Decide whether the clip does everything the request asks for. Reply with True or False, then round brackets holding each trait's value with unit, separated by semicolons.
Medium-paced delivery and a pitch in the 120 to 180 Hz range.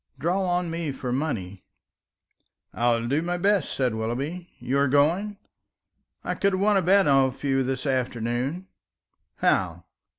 True (155 wpm; 140 Hz)